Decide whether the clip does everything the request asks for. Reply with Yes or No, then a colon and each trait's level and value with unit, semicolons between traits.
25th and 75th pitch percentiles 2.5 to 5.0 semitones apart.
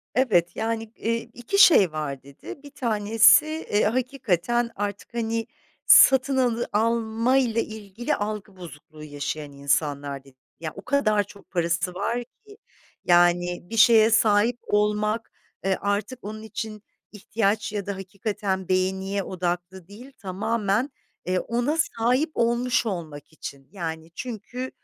Yes: average, 4.4 semitones